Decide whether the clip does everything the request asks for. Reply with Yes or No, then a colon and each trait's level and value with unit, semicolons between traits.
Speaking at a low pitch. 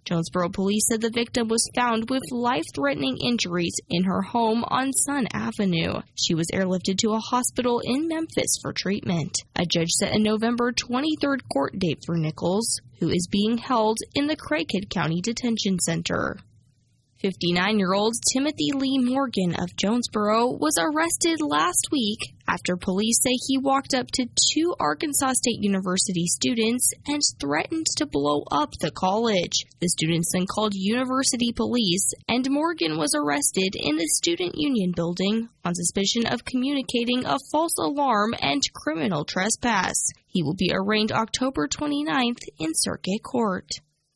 No: high, 220 Hz